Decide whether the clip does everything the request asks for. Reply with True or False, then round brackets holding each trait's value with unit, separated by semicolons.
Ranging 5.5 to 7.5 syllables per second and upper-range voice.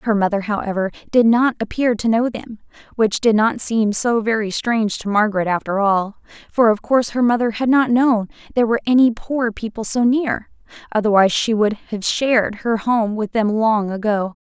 False (5.2 syllables/s; 220 Hz)